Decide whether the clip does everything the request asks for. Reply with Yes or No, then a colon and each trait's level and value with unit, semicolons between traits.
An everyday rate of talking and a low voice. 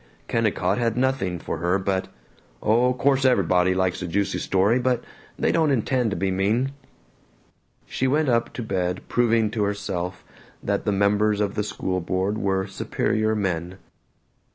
Yes: average, 155 wpm; low, 100 Hz